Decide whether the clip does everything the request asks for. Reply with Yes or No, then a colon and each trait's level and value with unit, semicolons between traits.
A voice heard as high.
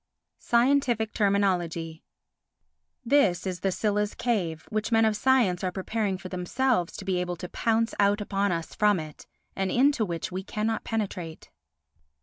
Yes: high, 200 Hz